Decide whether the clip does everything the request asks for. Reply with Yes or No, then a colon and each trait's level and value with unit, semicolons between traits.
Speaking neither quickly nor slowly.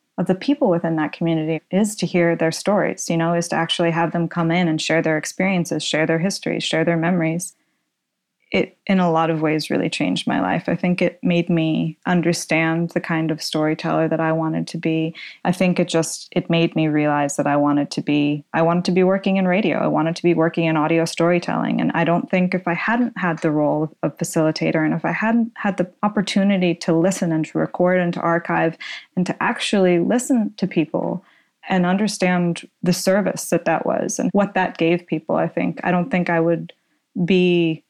No: fast, 215 wpm